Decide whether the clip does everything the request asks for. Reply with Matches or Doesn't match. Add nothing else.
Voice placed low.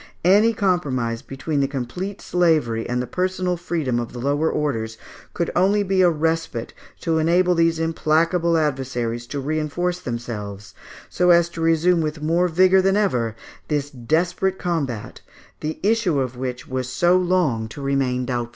Doesn't match